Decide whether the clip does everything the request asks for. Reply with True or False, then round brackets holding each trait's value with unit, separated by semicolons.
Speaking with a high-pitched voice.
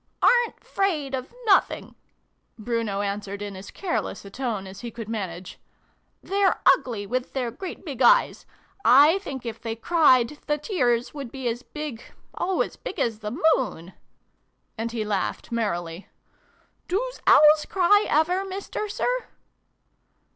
True (250 Hz)